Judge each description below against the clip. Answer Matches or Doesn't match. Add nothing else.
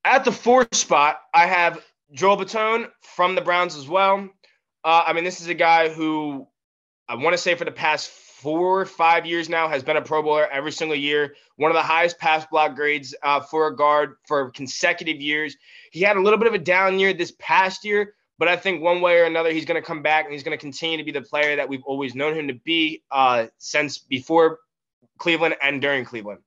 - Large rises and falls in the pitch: Doesn't match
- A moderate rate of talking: Doesn't match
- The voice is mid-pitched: Matches